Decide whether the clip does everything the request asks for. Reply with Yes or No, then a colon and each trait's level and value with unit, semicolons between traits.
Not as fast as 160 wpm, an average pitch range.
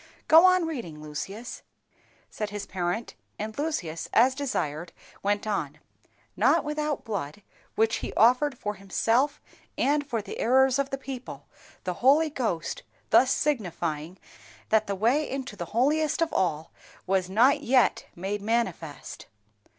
No: average, 140 wpm; wide, 6.5 semitones